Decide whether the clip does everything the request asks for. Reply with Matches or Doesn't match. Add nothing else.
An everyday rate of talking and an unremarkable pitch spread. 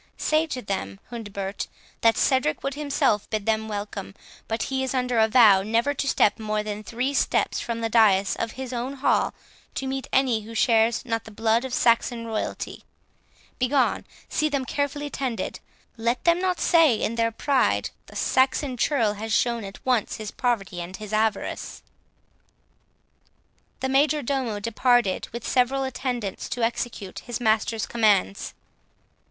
Matches